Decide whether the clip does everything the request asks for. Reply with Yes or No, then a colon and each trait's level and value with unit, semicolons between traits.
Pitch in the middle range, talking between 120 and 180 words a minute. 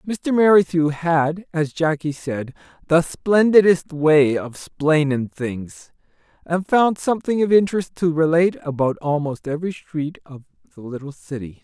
Yes: medium, 160 Hz; average, 140 wpm